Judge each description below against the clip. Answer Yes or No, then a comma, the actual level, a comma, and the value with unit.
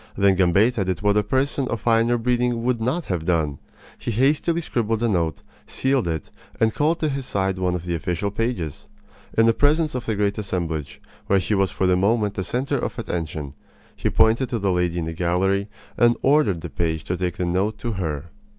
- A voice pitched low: Yes, low, 100 Hz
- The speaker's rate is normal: No, fast, 210 wpm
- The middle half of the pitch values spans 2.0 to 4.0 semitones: No, average, 5.2 semitones